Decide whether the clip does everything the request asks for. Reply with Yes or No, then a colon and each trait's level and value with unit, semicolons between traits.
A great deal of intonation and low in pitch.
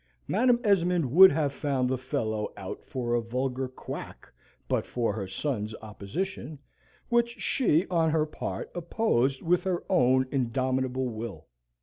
Yes: wide, 6.2 semitones; low, 130 Hz